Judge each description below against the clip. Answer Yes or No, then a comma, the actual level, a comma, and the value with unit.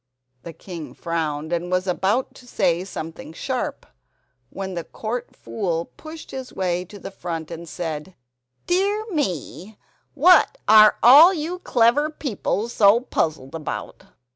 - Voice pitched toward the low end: No, high, 195 Hz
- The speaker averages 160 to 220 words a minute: No, average, 140 wpm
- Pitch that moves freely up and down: Yes, wide, 7.1 semitones